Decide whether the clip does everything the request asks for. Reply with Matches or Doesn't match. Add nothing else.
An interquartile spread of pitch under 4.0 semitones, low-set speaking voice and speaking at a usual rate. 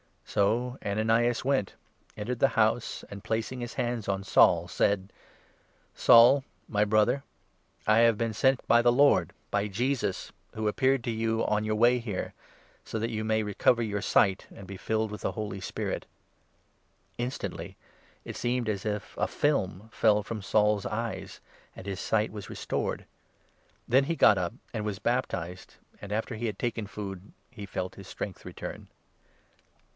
Matches